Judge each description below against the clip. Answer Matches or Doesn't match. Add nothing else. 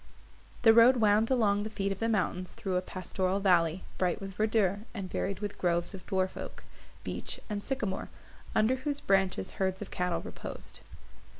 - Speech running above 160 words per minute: Matches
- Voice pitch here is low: Doesn't match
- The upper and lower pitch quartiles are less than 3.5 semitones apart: Matches